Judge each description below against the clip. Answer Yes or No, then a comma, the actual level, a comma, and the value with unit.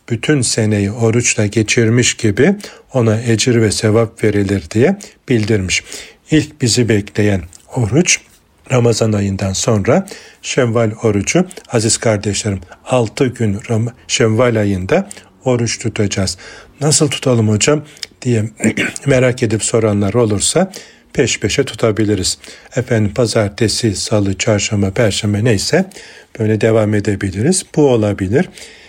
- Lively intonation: No, average, 2.8 semitones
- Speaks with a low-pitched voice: Yes, low, 110 Hz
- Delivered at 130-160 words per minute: No, average, 105 wpm